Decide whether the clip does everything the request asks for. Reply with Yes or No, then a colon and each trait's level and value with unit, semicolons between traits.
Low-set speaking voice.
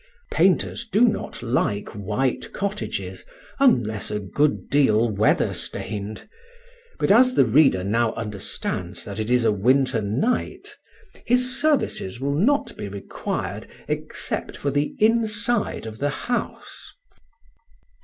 Yes: low, 130 Hz